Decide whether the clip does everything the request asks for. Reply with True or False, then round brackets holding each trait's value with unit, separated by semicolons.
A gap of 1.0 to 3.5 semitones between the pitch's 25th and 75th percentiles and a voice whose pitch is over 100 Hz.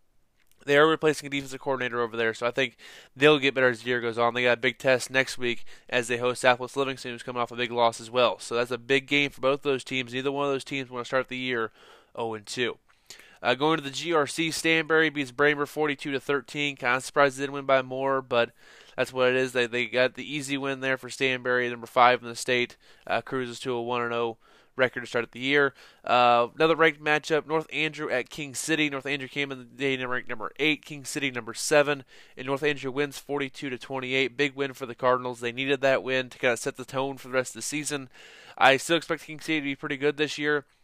True (2.6 semitones; 135 Hz)